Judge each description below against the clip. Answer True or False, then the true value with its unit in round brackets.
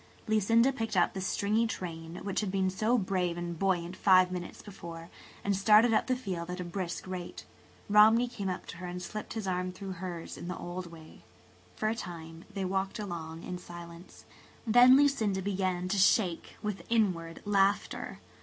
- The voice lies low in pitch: False (190 Hz)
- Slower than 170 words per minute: False (180 wpm)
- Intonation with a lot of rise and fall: False (3.2 semitones)